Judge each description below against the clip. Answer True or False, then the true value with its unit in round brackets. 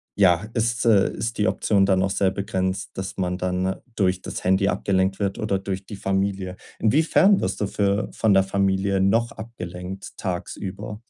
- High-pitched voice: False (95 Hz)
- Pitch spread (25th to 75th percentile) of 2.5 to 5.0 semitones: False (1.8 semitones)